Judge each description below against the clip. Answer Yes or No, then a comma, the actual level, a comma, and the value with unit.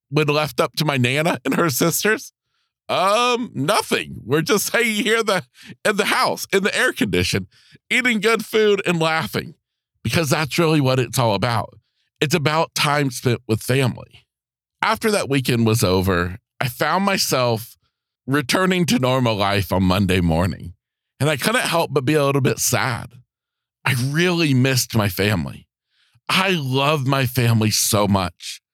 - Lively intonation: Yes, wide, 6.7 semitones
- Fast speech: No, average, 165 wpm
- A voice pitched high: No, medium, 140 Hz